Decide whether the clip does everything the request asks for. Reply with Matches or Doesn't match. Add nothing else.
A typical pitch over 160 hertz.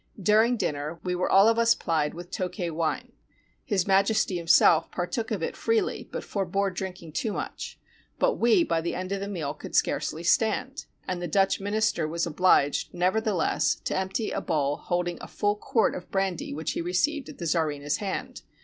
Matches